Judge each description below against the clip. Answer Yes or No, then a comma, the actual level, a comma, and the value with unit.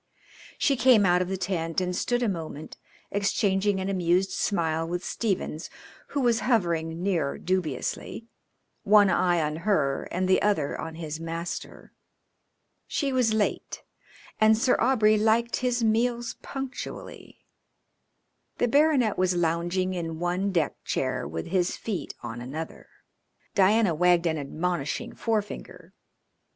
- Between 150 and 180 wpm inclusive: No, slow, 135 wpm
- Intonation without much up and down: No, average, 4.8 semitones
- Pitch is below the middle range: No, medium, 185 Hz